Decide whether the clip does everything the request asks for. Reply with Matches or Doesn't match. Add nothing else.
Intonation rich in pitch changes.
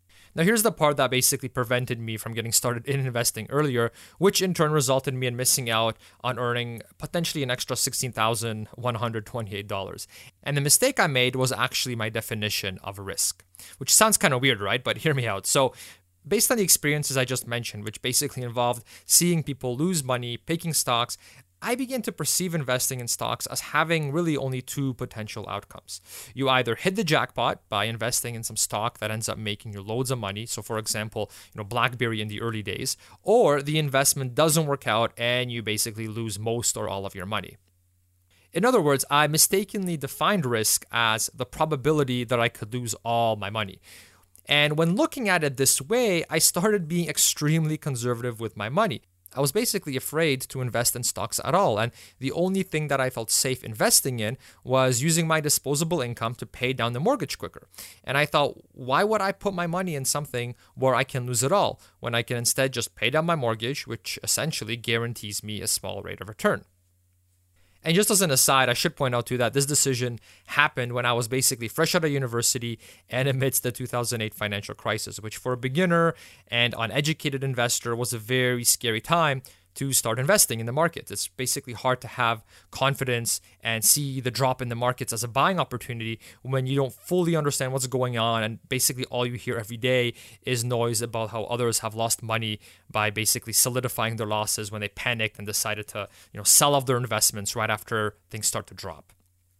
Doesn't match